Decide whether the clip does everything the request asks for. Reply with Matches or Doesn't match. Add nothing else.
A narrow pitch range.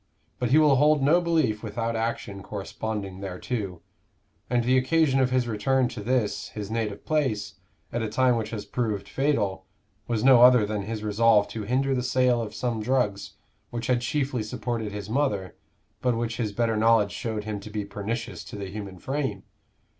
Doesn't match